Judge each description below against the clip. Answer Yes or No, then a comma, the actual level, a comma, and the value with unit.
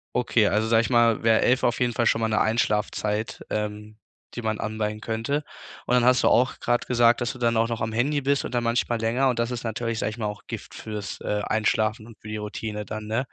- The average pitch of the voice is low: Yes, low, 115 Hz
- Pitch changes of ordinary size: No, narrow, 2.0 semitones